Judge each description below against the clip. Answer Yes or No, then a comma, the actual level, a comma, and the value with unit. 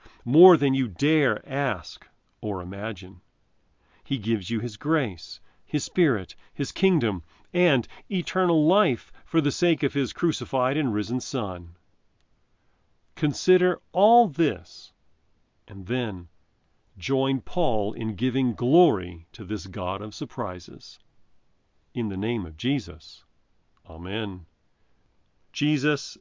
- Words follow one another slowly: Yes, slow, 115 wpm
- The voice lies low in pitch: Yes, low, 115 Hz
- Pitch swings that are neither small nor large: No, wide, 8.0 semitones